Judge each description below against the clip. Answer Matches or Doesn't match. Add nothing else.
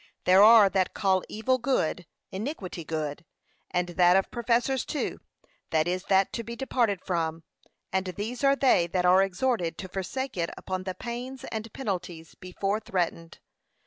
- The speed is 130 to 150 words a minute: Doesn't match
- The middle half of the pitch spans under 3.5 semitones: Doesn't match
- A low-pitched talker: Doesn't match